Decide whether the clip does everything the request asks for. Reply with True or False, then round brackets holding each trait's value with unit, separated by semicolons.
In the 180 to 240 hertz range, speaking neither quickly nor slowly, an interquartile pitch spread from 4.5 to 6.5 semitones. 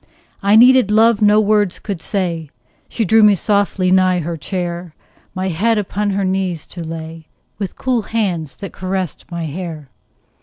False (190 Hz; 160 wpm; 3.5 semitones)